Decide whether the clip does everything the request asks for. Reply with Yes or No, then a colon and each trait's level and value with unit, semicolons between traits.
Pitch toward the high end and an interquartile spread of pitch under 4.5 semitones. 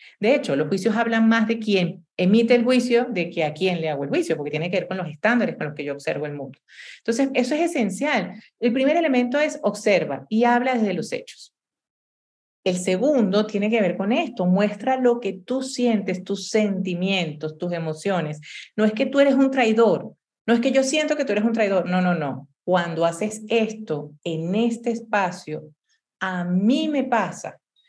No: high, 210 Hz; average, 5.1 semitones